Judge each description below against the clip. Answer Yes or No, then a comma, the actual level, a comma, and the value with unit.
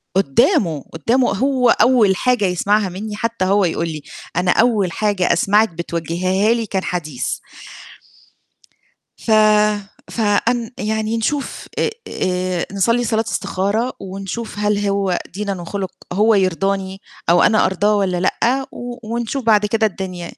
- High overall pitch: Yes, high, 200 Hz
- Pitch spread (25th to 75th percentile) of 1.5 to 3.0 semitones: No, average, 3.4 semitones